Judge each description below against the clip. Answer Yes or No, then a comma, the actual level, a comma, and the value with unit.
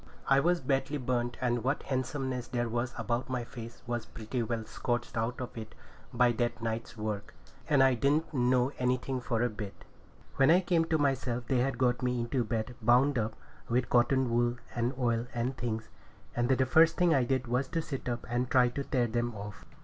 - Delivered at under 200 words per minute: No, fast, 205 wpm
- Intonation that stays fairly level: Yes, narrow, 2.0 semitones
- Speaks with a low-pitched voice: Yes, low, 125 Hz